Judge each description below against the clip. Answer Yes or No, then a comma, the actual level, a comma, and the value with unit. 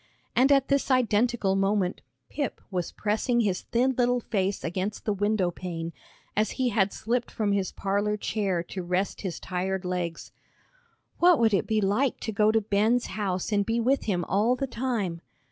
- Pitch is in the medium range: No, high, 210 Hz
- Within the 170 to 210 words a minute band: Yes, average, 180 wpm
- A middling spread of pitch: Yes, average, 3.8 semitones